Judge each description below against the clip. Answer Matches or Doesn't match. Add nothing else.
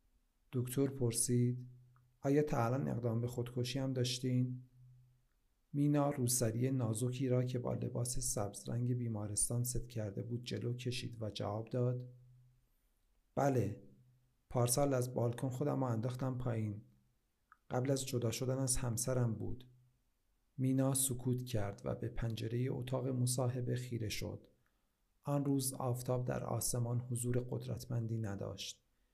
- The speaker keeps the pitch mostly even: Matches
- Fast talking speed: Doesn't match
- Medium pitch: Doesn't match